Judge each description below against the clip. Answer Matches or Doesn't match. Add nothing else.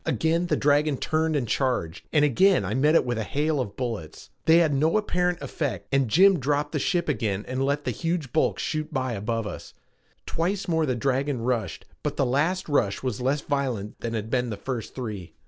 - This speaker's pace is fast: Matches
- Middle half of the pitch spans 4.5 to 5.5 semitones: Matches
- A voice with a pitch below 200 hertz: Matches